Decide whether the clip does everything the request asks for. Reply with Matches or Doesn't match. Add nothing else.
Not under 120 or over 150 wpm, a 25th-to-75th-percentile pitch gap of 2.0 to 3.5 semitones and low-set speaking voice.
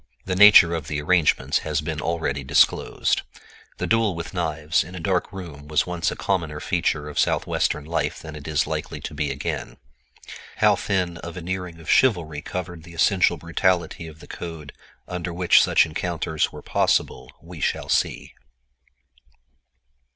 Doesn't match